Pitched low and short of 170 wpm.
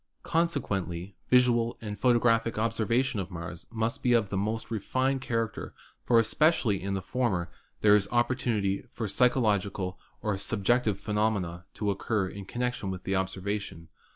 Yes: low, 110 Hz; average, 145 wpm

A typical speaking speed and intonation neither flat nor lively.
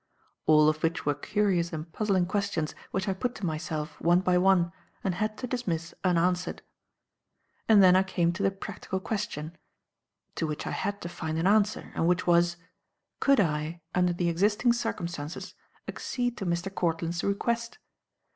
Yes: average, 165 wpm; average, 3.2 semitones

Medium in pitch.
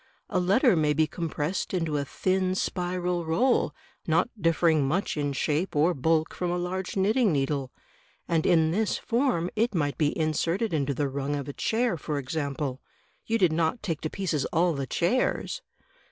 Yes: medium, 165 Hz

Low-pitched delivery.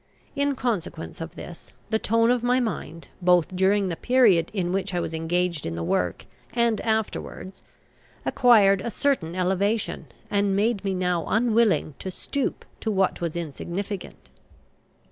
No: high, 195 Hz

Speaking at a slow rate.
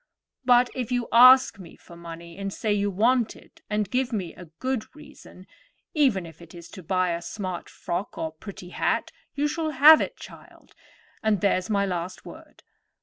No: average, 175 wpm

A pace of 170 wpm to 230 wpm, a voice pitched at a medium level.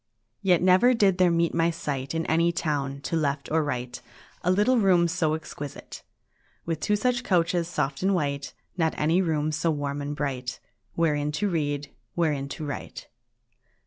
Yes: average, 175 wpm; medium, 160 Hz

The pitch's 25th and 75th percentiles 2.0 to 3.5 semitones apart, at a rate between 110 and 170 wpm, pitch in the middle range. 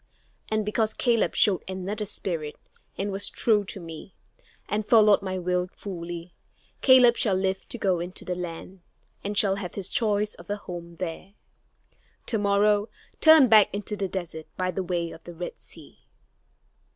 No: average, 2.8 semitones; average, 165 wpm; high, 195 Hz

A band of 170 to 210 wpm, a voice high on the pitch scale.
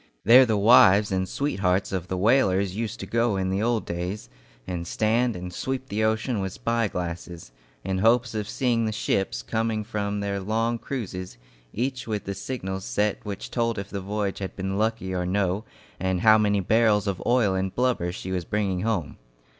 No: average, 195 wpm; low, 100 Hz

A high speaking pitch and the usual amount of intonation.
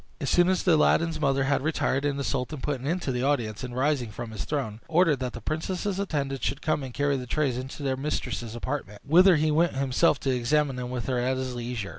No: low, 135 Hz; average, 3.3 semitones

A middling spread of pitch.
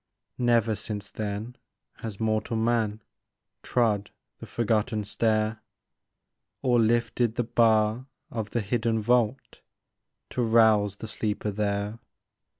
No: narrow, 1.8 semitones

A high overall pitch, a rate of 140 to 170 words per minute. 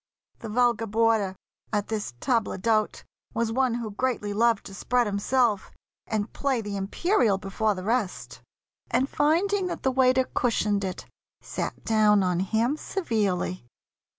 Yes: high, 225 Hz; average, 145 wpm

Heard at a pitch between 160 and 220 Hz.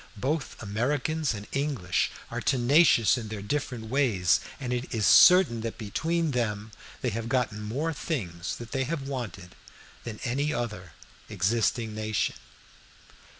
No: low, 120 Hz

